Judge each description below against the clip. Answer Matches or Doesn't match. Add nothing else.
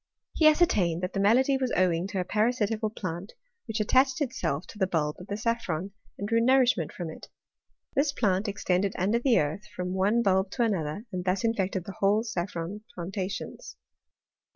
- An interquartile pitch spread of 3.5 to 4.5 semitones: Matches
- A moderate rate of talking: Matches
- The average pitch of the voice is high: Matches